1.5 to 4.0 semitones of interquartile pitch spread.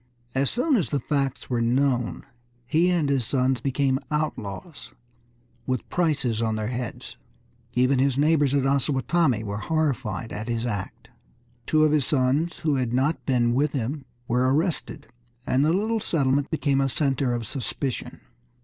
Yes: average, 3.6 semitones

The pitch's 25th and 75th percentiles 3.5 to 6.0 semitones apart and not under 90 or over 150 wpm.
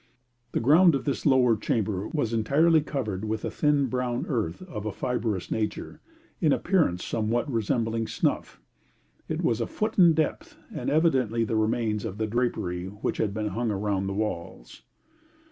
No: average, 4.6 semitones; average, 165 wpm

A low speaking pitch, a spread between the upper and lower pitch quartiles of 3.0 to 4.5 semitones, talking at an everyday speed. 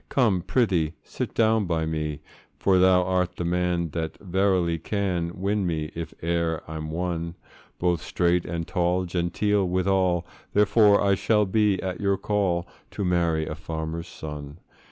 No: very low, 90 Hz; narrow, 2.6 semitones; average, 155 wpm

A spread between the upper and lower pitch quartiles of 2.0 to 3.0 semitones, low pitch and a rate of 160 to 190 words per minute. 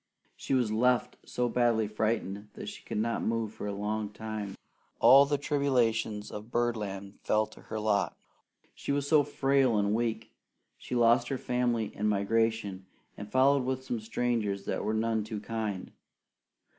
Yes: average, 2.7 semitones; low, 110 Hz; average, 165 wpm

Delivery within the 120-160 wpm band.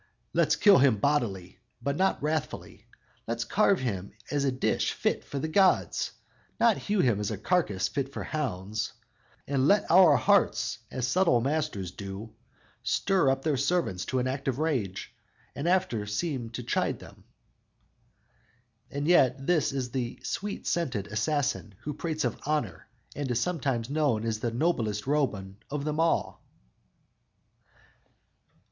Yes: average, 150 wpm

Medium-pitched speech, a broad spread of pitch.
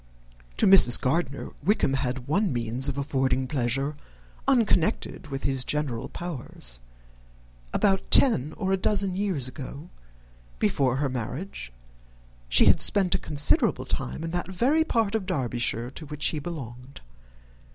Yes: medium, 145 Hz; wide, 6.3 semitones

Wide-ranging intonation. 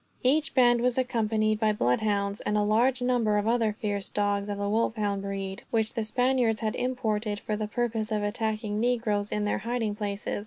No: narrow, 2.4 semitones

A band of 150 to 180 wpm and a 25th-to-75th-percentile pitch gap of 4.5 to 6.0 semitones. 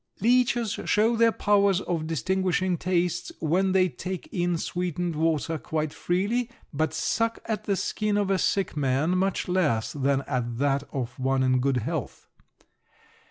Yes: average, 155 wpm; average, 5.2 semitones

